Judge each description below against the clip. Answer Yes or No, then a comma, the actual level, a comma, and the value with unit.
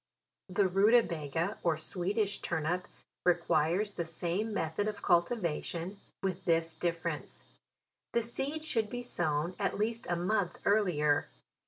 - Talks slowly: Yes, slow, 130 wpm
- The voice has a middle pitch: Yes, medium, 180 Hz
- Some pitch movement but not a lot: Yes, average, 4.1 semitones